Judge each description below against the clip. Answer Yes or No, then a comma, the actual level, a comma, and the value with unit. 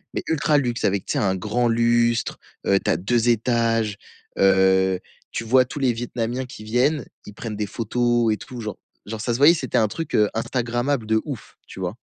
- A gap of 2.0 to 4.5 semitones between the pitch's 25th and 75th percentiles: Yes, narrow, 2.5 semitones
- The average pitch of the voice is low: Yes, low, 115 Hz